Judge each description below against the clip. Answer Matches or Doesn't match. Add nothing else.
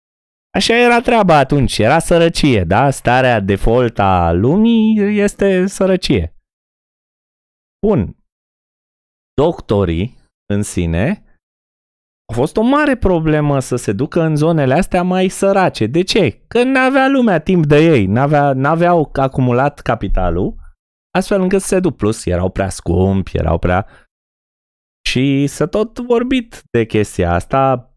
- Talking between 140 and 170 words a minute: Doesn't match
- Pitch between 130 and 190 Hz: Matches